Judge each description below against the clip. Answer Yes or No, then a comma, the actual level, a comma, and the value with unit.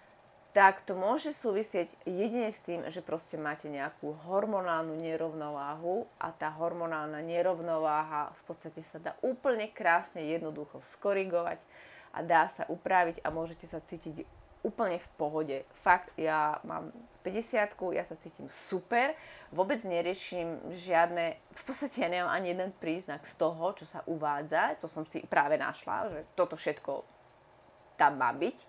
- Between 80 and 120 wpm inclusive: No, average, 145 wpm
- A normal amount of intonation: Yes, average, 3.6 semitones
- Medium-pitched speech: Yes, medium, 170 Hz